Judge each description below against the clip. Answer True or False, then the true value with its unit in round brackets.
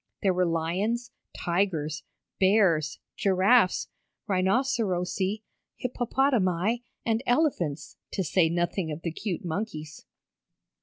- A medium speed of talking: False (95 wpm)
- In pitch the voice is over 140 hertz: True (185 Hz)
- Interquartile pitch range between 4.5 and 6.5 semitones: True (4.8 semitones)